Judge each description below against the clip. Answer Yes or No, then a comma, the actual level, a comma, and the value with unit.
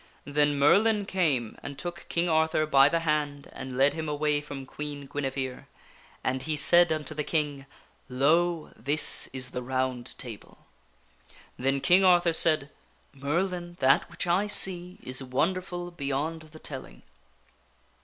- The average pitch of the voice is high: No, medium, 150 Hz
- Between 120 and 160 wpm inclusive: Yes, average, 150 wpm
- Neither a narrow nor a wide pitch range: Yes, average, 4.0 semitones